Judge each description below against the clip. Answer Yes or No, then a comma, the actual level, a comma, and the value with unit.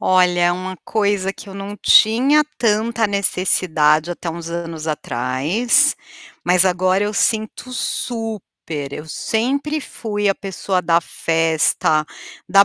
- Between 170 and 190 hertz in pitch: Yes, medium, 185 Hz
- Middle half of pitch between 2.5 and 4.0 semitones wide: No, average, 4.5 semitones